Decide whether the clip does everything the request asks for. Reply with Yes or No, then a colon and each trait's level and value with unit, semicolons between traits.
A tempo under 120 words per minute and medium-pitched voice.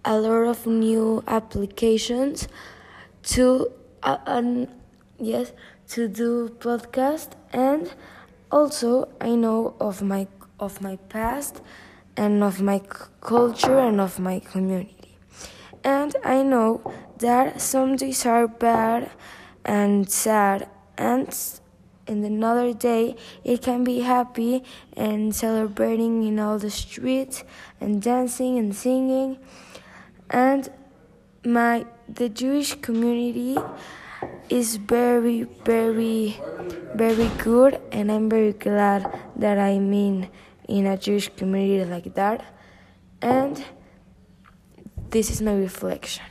No: average, 110 wpm; high, 230 Hz